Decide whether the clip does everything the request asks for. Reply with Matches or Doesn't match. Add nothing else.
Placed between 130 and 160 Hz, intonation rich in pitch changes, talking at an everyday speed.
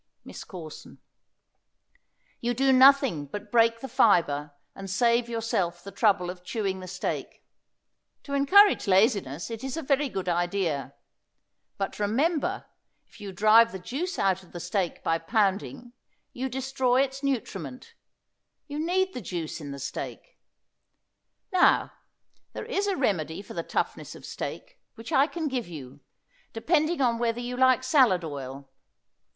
Doesn't match